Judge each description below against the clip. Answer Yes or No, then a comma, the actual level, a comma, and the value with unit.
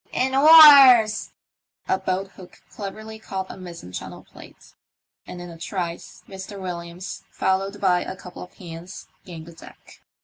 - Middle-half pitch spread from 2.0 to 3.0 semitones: Yes, average, 2.7 semitones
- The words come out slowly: No, average, 165 wpm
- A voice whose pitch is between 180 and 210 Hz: Yes, high, 190 Hz